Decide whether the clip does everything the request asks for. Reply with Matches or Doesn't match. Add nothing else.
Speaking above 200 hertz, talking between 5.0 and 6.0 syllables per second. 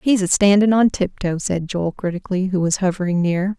Doesn't match